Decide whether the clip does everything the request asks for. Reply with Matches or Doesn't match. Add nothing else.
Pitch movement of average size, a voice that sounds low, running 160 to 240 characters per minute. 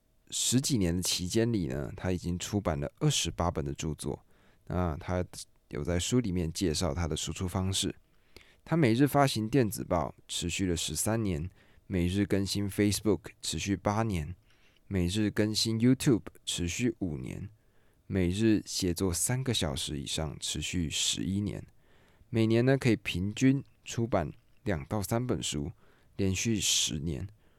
Doesn't match